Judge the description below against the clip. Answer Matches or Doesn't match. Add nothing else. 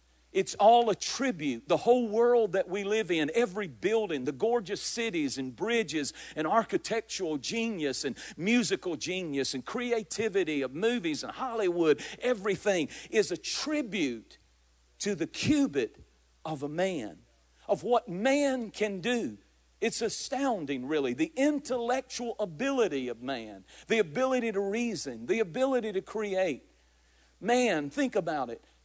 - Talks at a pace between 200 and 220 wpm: Doesn't match